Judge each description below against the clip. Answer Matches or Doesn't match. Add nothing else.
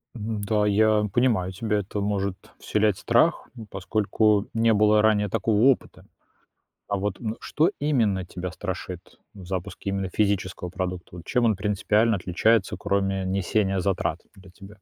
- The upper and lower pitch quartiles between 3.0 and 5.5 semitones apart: Doesn't match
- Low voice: Matches